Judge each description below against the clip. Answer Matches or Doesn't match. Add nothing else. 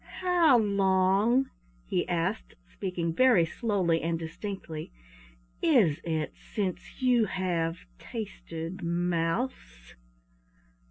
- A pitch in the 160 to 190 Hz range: Matches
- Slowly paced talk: Matches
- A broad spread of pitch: Doesn't match